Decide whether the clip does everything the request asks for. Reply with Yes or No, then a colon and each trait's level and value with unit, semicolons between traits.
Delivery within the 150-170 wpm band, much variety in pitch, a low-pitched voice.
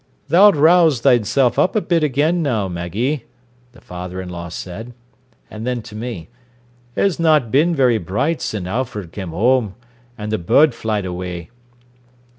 Yes: average, 155 wpm; wide, 7.6 semitones; low, 115 Hz